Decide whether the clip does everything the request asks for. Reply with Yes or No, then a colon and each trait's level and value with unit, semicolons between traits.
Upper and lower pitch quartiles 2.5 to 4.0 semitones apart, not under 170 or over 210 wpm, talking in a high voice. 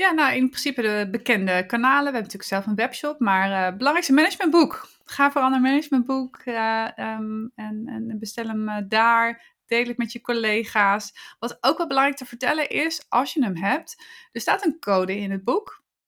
No: average, 4.6 semitones; fast, 200 wpm; high, 240 Hz